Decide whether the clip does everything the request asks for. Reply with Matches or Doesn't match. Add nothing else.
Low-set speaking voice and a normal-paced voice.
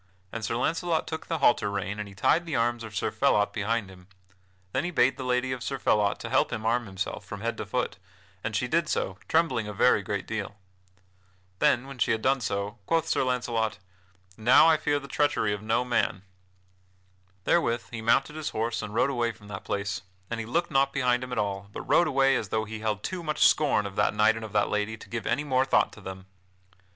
Doesn't match